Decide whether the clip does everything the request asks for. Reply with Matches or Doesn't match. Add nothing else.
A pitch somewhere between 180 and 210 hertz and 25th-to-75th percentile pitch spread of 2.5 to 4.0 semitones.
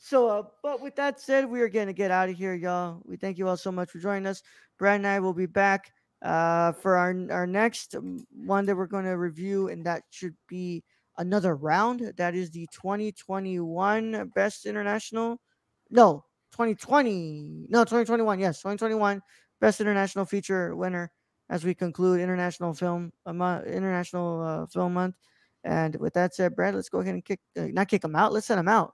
Matches